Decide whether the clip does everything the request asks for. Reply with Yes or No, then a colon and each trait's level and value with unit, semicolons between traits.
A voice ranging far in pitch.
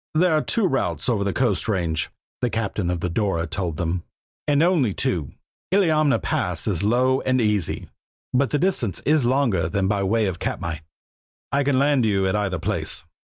Yes: wide, 7.3 semitones